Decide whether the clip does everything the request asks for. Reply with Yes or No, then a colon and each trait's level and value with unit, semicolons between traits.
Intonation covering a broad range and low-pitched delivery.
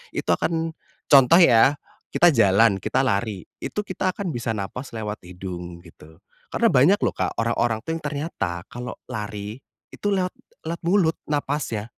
Yes: wide, 7.9 semitones; low, 120 Hz